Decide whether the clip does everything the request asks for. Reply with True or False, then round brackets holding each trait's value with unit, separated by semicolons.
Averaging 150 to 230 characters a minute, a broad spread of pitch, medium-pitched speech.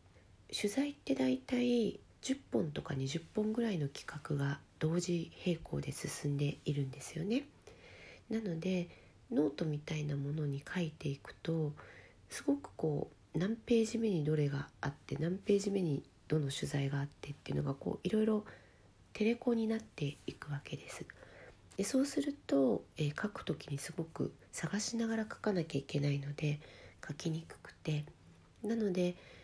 False (300 characters per minute; 6.3 semitones; 155 Hz)